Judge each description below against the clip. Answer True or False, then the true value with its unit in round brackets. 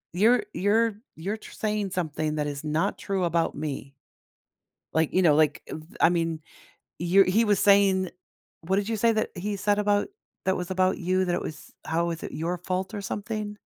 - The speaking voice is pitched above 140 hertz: True (185 Hz)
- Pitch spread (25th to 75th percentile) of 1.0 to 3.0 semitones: False (3.7 semitones)